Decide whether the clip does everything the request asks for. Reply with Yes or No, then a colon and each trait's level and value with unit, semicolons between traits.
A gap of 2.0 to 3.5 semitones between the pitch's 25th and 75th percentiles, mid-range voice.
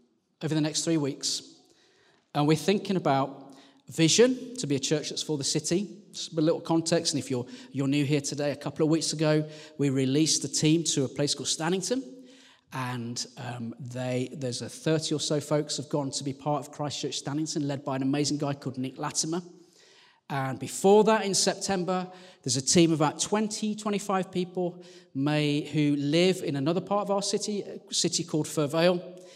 No: average, 4.3 semitones; medium, 155 Hz